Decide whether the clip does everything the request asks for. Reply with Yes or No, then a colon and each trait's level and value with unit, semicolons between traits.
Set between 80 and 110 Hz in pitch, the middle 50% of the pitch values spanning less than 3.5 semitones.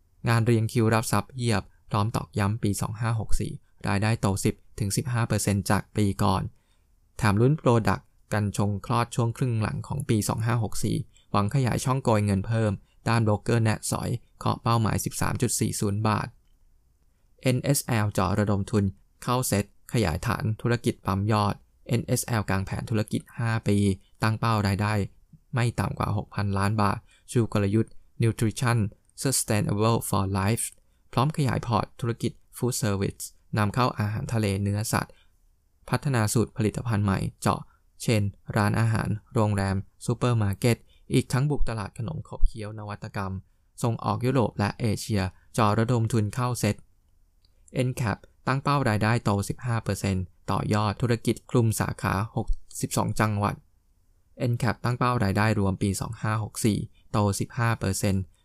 Yes: low, 105 Hz; average, 3.0 semitones